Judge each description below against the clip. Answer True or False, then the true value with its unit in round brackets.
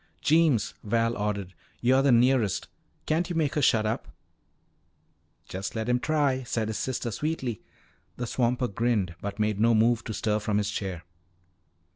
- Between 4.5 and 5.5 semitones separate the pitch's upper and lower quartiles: False (3.8 semitones)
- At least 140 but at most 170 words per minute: True (160 wpm)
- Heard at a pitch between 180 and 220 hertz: False (115 Hz)